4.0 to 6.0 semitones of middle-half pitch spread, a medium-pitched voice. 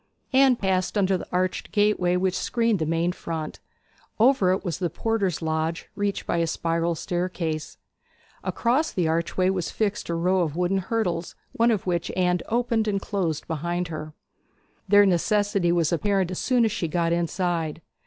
No: average, 3.4 semitones; medium, 180 Hz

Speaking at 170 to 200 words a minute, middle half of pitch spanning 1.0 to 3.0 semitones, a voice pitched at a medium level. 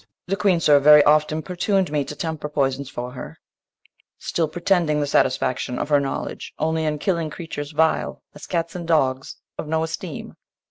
Yes: average, 175 wpm; narrow, 2.5 semitones; medium, 155 Hz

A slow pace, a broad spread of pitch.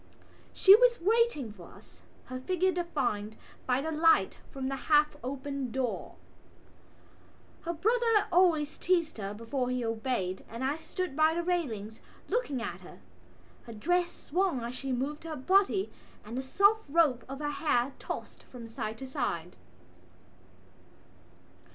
No: average, 145 wpm; wide, 6.1 semitones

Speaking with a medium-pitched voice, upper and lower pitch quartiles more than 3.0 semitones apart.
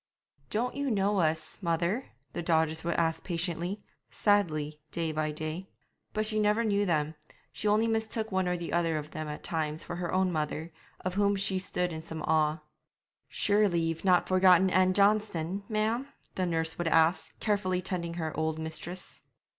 Yes: medium, 175 Hz; average, 3.9 semitones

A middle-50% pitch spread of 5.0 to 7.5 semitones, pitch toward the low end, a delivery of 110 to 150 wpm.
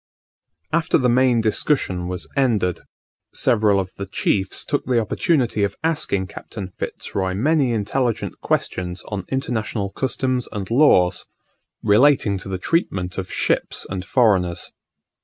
Yes: average, 5.3 semitones; low, 105 Hz; slow, 135 wpm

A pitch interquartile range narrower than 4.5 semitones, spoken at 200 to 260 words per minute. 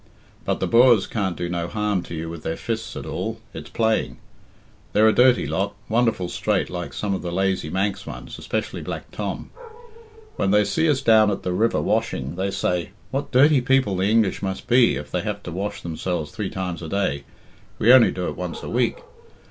Yes: average, 4.1 semitones; fast, 205 wpm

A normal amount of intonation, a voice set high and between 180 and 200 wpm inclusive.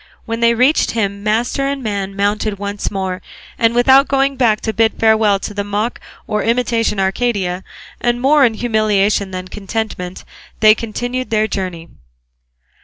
No: average, 3.1 semitones; high, 215 Hz; average, 155 wpm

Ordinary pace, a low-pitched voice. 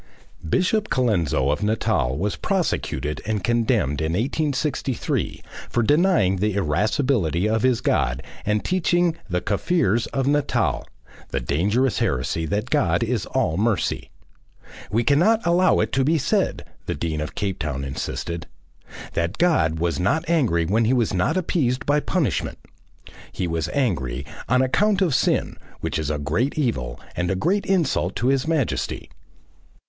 Yes: average, 150 wpm; low, 110 Hz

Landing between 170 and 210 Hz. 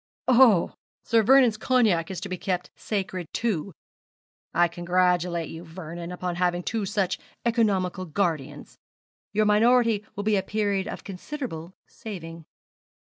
Yes: high, 190 Hz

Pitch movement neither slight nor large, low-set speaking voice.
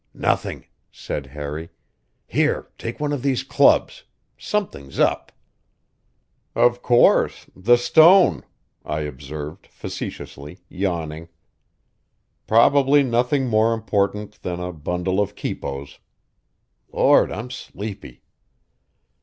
No: wide, 7.9 semitones; low, 100 Hz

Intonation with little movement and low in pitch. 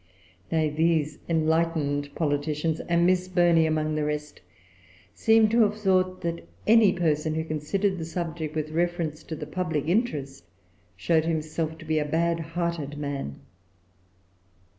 No: narrow, 2.2 semitones; medium, 160 Hz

